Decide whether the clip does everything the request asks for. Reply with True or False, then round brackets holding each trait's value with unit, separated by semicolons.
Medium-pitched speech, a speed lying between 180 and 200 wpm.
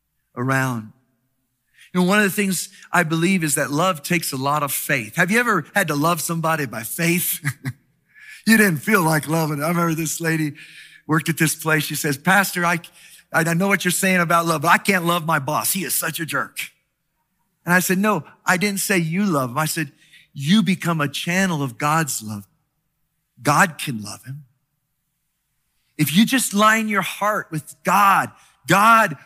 True (160 Hz; 190 wpm)